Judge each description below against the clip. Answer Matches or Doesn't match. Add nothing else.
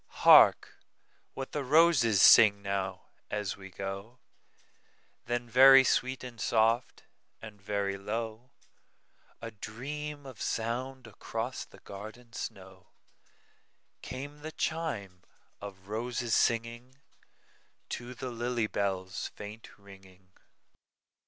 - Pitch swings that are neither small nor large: Matches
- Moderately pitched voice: Doesn't match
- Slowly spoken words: Matches